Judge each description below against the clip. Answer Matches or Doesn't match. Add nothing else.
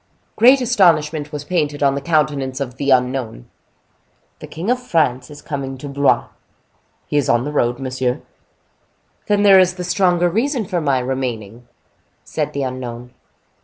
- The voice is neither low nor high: Matches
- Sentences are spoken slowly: Doesn't match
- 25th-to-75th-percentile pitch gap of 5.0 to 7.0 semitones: Matches